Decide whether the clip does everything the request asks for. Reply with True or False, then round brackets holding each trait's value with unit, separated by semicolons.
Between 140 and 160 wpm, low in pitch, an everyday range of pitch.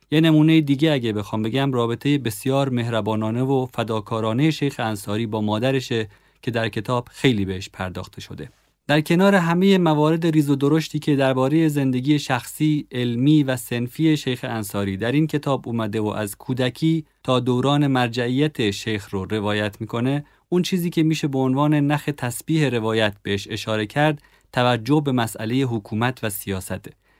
True (155 wpm; 130 Hz; 5.0 semitones)